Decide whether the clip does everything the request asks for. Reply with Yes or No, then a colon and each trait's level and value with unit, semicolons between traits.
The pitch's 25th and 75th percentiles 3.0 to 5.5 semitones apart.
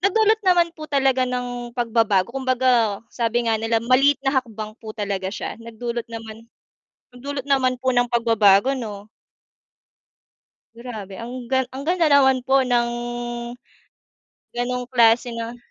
No: narrow, 2.5 semitones